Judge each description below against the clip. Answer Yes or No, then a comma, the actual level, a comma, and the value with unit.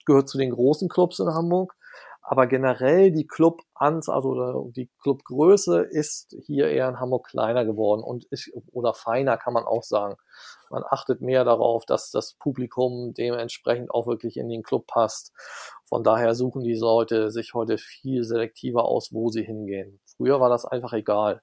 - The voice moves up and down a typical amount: Yes, average, 3.1 semitones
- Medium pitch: No, low, 125 Hz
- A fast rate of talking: No, average, 170 wpm